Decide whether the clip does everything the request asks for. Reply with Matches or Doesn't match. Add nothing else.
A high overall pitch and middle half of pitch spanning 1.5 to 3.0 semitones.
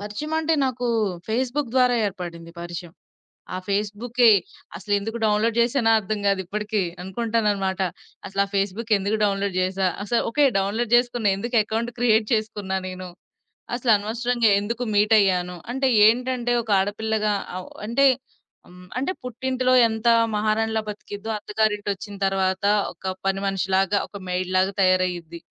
Doesn't match